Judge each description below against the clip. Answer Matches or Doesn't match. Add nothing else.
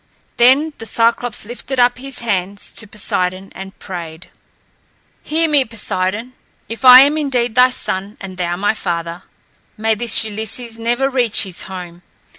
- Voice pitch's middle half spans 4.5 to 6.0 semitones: Matches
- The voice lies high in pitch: Matches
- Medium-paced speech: Matches